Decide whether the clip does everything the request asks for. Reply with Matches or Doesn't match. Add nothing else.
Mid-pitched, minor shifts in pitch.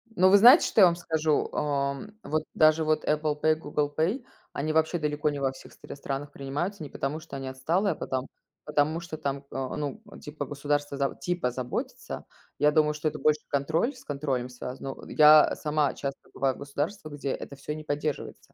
Matches